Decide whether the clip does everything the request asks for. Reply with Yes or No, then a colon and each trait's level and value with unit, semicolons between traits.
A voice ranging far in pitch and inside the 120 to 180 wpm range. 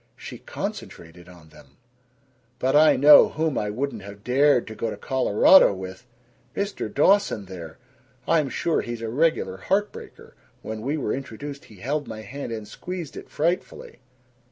Yes: wide, 6.5 semitones; average, 160 wpm